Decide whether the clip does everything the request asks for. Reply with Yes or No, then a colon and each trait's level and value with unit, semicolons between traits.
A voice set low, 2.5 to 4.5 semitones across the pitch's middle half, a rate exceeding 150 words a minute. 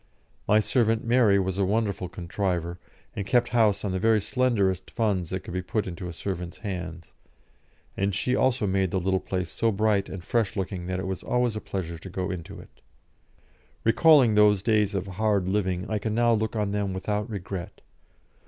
Yes: low, 100 Hz; average, 2.9 semitones; average, 190 wpm